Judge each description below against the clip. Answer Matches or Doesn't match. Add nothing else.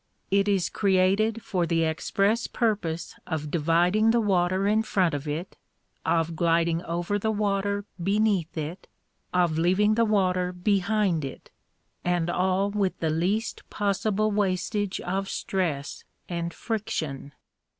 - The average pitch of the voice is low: Doesn't match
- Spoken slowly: Matches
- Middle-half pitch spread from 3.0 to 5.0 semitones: Matches